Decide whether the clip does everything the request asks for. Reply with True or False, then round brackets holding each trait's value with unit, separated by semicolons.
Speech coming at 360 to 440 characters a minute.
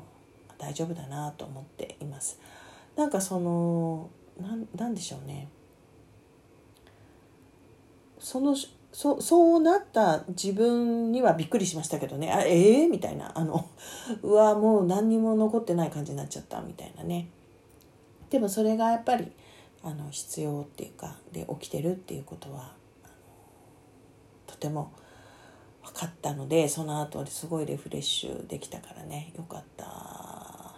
False (285 characters per minute)